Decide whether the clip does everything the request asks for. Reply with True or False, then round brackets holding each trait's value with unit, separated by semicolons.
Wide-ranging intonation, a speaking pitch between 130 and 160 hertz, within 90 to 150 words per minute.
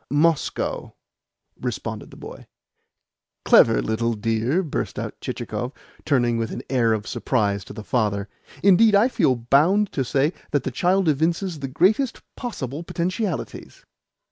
True (7.5 semitones; 140 Hz; 140 wpm)